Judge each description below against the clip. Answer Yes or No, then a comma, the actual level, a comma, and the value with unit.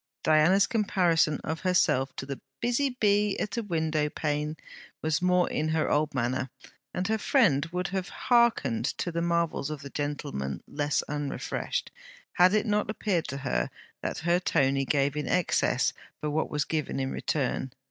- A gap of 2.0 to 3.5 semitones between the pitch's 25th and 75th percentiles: No, average, 4.4 semitones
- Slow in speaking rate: No, average, 170 wpm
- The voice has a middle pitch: Yes, medium, 160 Hz